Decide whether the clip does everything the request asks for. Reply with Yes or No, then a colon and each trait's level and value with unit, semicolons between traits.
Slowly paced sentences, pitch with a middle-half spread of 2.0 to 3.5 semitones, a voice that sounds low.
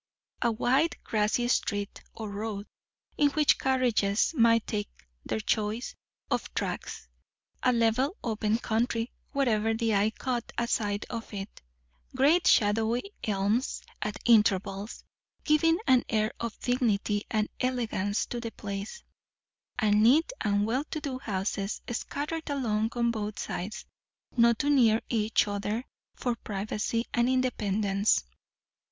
No: slow, 130 wpm; average, 3.1 semitones; high, 225 Hz